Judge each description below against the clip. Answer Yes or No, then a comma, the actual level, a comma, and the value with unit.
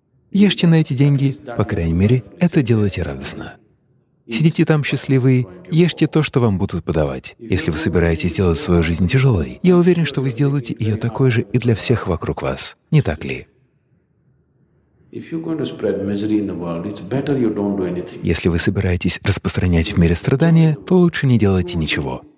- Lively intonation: Yes, wide, 7.9 semitones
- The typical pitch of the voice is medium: No, low, 115 Hz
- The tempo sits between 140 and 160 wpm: Yes, average, 145 wpm